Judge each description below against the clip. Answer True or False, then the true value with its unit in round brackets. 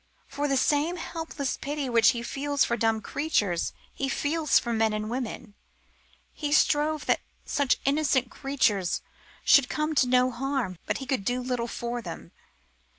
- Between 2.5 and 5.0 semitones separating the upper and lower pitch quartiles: True (3.7 semitones)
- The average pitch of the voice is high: True (260 Hz)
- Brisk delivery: False (160 wpm)